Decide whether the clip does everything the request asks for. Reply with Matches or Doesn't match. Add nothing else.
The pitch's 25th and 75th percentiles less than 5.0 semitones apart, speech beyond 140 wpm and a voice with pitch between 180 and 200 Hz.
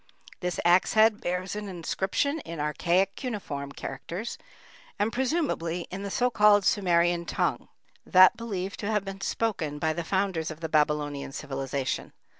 Matches